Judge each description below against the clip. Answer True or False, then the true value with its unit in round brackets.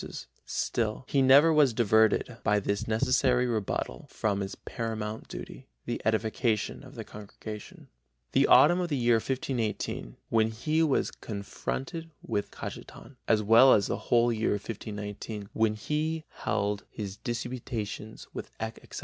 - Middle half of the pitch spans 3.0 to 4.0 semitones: True (3.3 semitones)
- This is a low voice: True (110 Hz)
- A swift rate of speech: False (150 wpm)